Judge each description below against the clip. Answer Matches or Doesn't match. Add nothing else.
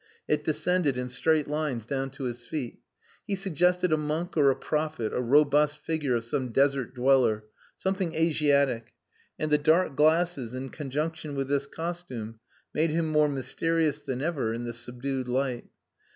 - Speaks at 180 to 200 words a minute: Doesn't match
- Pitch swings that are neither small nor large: Matches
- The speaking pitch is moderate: Matches